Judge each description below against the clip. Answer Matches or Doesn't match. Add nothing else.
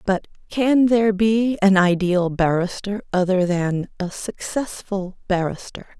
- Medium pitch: Doesn't match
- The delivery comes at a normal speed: Doesn't match